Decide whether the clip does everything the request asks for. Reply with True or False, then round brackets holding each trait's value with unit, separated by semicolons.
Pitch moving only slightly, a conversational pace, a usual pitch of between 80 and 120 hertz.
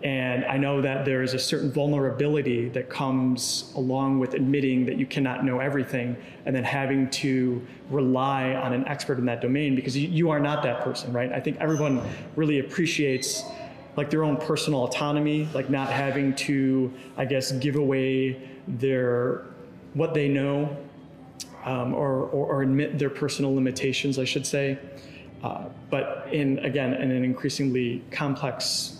False (1.7 semitones; 160 wpm; 135 Hz)